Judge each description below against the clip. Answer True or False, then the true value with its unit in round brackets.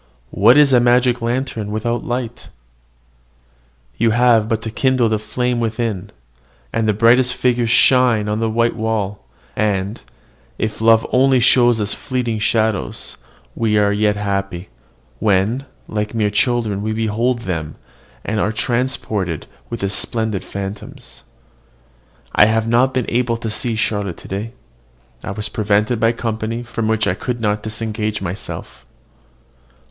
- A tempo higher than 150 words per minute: False (145 wpm)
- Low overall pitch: True (110 Hz)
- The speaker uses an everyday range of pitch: False (2.3 semitones)